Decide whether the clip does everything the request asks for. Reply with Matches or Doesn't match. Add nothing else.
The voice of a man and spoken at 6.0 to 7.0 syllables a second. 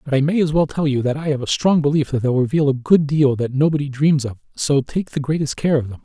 Matches